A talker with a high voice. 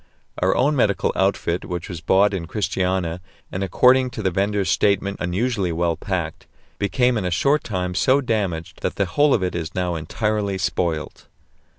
No: very low, 95 Hz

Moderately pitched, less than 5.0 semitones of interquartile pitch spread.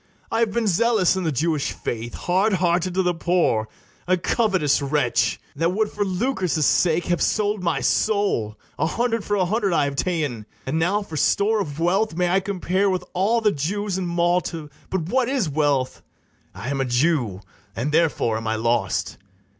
No: medium, 175 Hz; wide, 5.5 semitones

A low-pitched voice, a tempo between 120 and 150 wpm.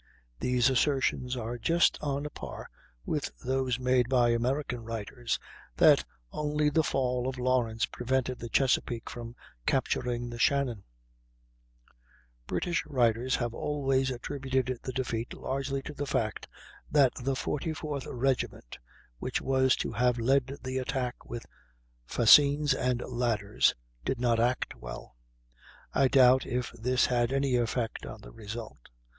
Yes: low, 125 Hz; slow, 135 wpm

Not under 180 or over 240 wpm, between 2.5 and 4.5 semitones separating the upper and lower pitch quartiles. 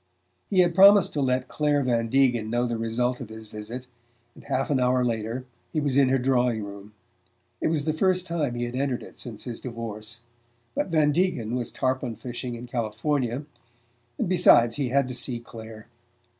Yes: average, 190 wpm; average, 3.4 semitones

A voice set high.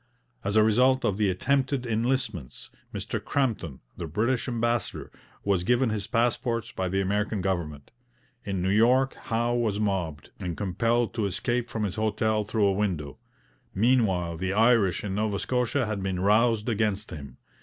No: low, 105 Hz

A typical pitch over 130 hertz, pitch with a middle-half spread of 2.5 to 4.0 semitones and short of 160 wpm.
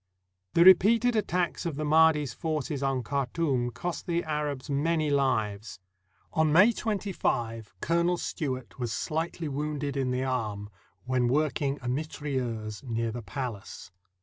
No: medium, 140 Hz; average, 4.6 semitones; average, 145 wpm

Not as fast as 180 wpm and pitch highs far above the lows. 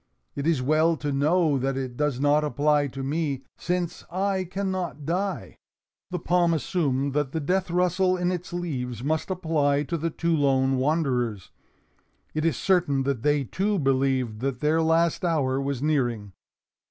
No: average, 165 wpm; average, 4.1 semitones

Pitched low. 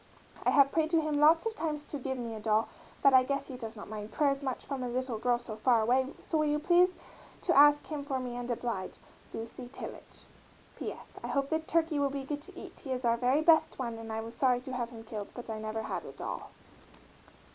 No: very high, 260 Hz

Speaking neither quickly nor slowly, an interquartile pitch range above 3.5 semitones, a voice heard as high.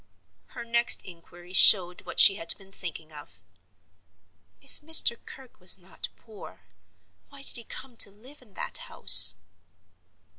Yes: average, 145 wpm; average, 5.3 semitones; high, 195 Hz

